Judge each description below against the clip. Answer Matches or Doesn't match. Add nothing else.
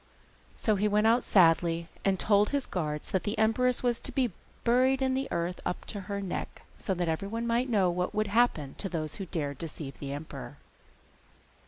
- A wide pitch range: Matches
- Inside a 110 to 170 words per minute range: Doesn't match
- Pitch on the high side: Matches